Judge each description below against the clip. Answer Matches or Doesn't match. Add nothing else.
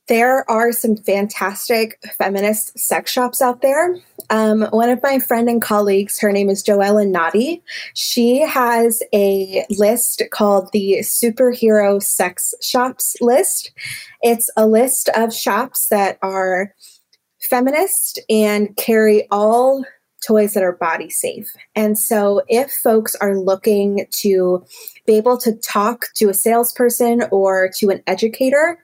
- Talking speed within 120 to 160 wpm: Matches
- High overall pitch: Matches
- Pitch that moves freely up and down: Doesn't match